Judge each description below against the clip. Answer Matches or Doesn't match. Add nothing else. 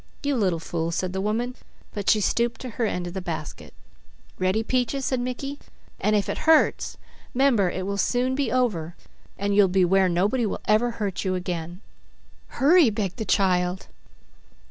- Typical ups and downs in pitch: Matches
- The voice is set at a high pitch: Matches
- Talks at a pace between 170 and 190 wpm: Matches